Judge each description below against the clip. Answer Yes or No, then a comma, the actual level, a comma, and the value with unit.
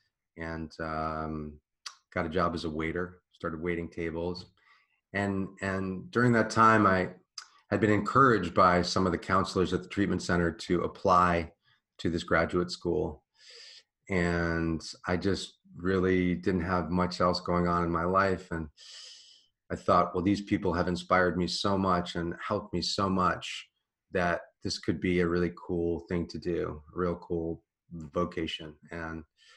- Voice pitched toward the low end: Yes, very low, 90 Hz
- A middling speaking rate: Yes, average, 160 wpm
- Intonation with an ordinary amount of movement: No, narrow, 2.1 semitones